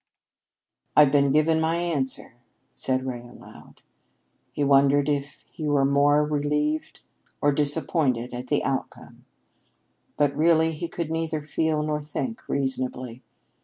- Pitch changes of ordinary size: No, narrow, 2.3 semitones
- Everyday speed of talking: No, slow, 130 wpm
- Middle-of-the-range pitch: Yes, medium, 145 Hz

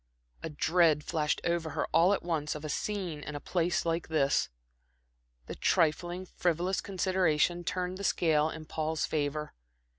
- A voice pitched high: No, medium, 165 Hz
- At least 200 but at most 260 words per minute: No, average, 155 wpm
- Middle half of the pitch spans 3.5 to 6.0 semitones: No, average, 2.8 semitones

